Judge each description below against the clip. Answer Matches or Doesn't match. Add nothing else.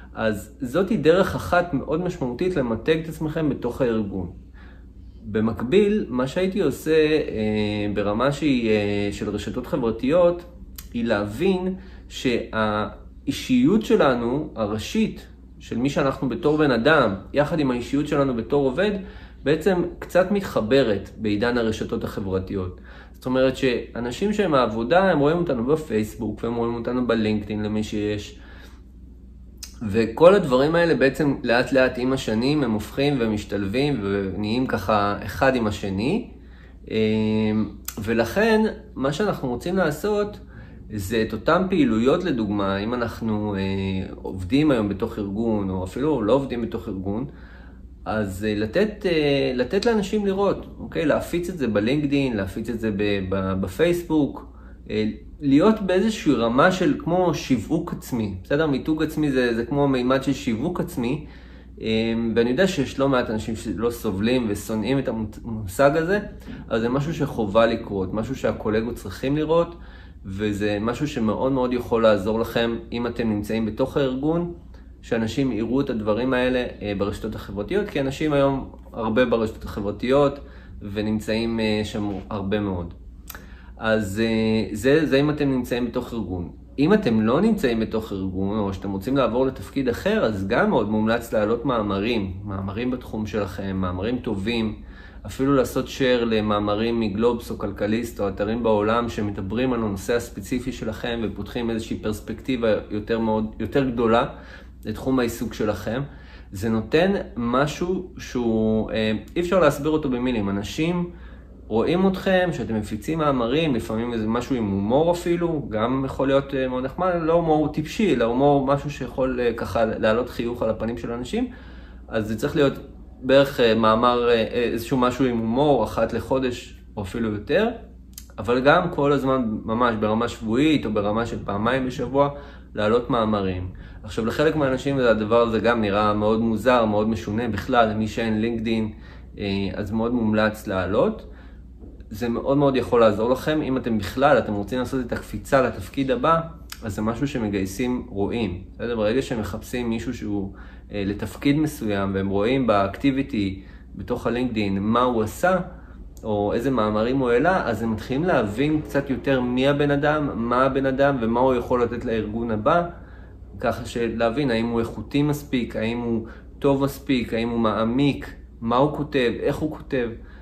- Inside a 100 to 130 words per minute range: Doesn't match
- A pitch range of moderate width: Matches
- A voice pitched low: Matches